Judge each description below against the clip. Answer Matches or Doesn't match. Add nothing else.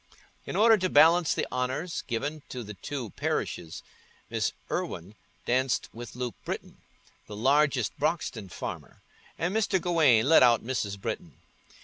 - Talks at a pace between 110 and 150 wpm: Matches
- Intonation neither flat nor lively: Doesn't match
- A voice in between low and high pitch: Doesn't match